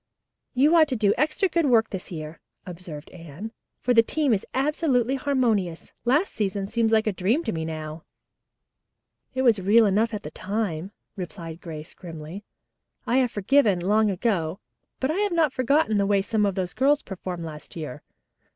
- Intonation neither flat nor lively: No, wide, 6.3 semitones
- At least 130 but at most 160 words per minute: No, average, 170 wpm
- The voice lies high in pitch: Yes, high, 210 Hz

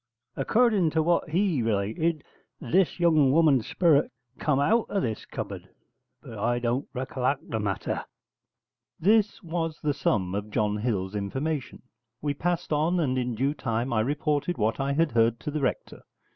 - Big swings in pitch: Yes, wide, 6.0 semitones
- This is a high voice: No, medium, 140 Hz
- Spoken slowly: No, average, 160 wpm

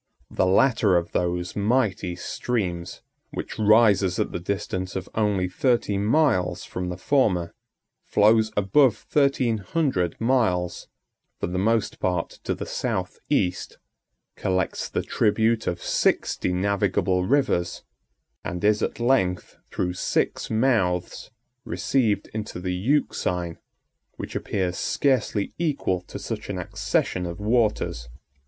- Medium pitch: No, low, 100 Hz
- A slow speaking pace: Yes, slow, 125 wpm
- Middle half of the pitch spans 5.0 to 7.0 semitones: No, average, 4.2 semitones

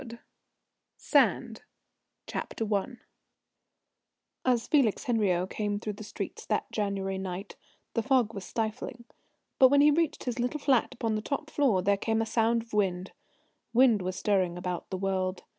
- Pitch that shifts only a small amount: No, average, 4.2 semitones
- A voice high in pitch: Yes, high, 215 Hz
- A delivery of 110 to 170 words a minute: Yes, average, 150 wpm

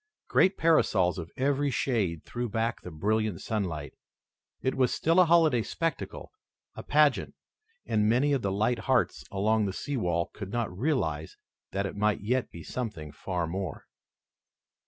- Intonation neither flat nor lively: No, wide, 6.1 semitones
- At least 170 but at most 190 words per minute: No, average, 155 wpm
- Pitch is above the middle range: No, low, 110 Hz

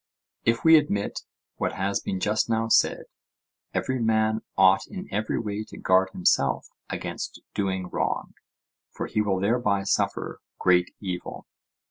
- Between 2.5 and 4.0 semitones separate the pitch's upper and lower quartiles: Yes, average, 2.9 semitones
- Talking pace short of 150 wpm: Yes, average, 140 wpm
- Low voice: Yes, low, 100 Hz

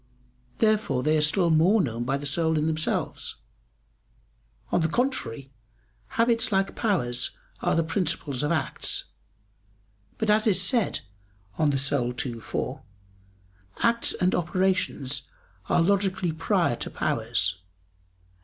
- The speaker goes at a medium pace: No, slow, 125 wpm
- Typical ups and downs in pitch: No, wide, 6.0 semitones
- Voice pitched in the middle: Yes, medium, 160 Hz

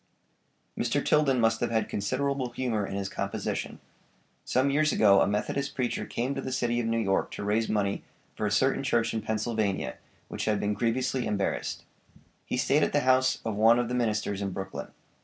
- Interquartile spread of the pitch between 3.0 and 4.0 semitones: Yes, average, 3.7 semitones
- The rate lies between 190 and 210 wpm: Yes, average, 195 wpm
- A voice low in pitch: Yes, low, 115 Hz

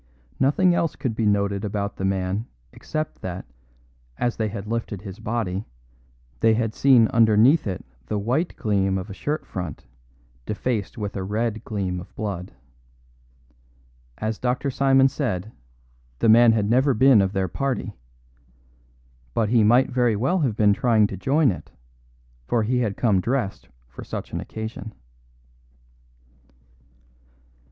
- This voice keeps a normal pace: Yes, average, 145 wpm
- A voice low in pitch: Yes, low, 110 Hz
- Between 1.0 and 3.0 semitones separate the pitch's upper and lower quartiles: No, average, 3.7 semitones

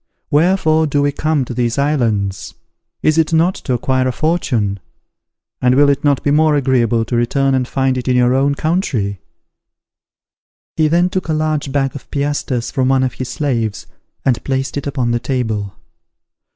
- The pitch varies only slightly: No, average, 3.4 semitones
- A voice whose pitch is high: No, low, 135 Hz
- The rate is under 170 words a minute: No, average, 180 wpm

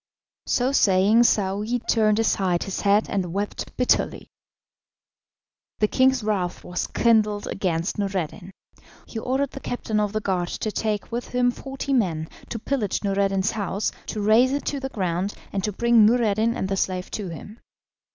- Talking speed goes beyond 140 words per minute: Yes, average, 160 wpm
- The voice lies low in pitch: No, high, 210 Hz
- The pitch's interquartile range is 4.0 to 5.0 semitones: No, average, 3.5 semitones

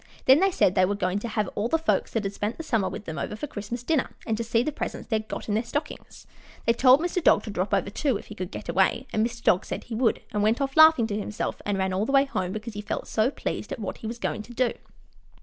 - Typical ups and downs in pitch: Yes, average, 3.8 semitones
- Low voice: No, high, 220 Hz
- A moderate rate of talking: No, fast, 295 wpm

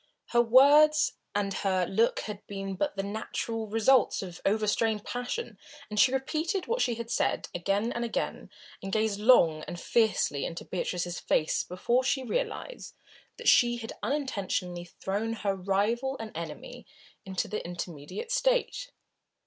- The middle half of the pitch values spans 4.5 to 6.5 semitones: Yes, average, 5.0 semitones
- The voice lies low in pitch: No, high, 220 Hz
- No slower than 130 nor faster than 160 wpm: Yes, average, 150 wpm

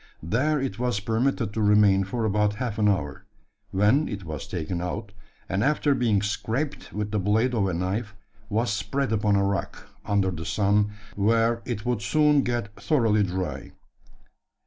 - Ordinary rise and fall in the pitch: Yes, average, 3.1 semitones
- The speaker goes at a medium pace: Yes, average, 170 wpm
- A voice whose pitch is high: No, low, 105 Hz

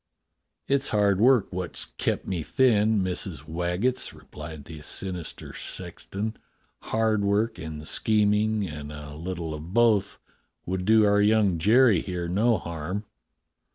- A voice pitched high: No, low, 100 Hz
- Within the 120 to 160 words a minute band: Yes, slow, 135 wpm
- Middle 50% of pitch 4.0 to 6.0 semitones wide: Yes, average, 4.6 semitones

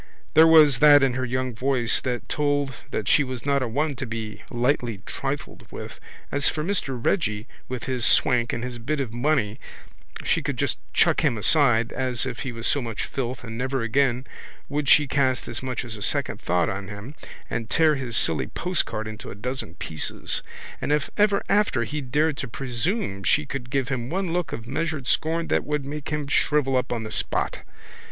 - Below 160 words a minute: No, average, 200 wpm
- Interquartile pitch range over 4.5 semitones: No, average, 3.8 semitones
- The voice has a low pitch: Yes, low, 130 Hz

